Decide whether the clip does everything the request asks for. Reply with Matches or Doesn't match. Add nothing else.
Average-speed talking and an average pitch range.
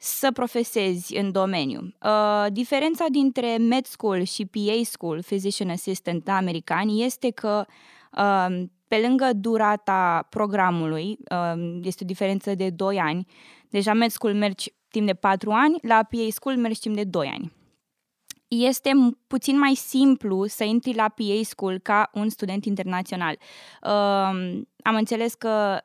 Matches